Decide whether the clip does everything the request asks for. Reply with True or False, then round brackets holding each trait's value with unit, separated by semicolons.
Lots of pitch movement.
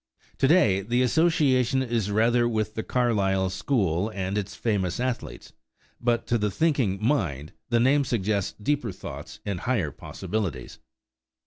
False (4.6 semitones)